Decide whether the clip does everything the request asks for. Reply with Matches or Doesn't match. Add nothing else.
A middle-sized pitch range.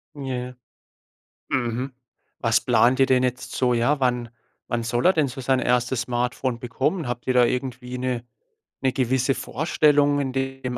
Doesn't match